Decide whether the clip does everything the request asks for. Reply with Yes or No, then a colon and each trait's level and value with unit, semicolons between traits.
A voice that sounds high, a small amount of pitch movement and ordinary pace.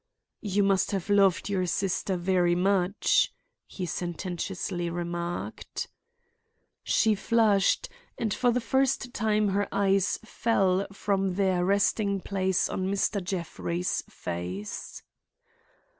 No: high, 195 Hz; narrow, 2.2 semitones; slow, 110 wpm